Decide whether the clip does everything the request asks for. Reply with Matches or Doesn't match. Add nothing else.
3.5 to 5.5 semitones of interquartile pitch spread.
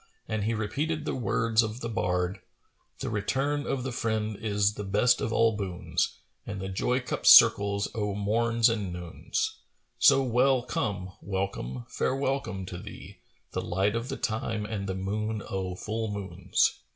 Doesn't match